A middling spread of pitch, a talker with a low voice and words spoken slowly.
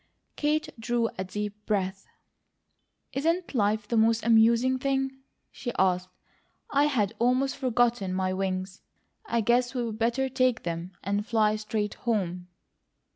No: average, 4.0 semitones; high, 225 Hz; slow, 130 wpm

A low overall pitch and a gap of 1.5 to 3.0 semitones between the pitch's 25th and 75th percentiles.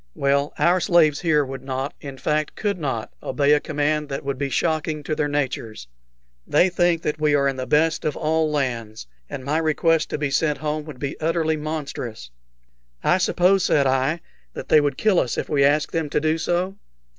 No: medium, 150 Hz; narrow, 2.5 semitones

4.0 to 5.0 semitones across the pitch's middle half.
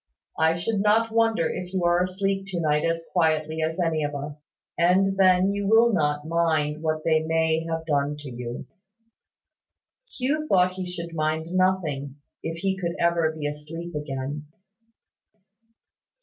No: average, 3.2 semitones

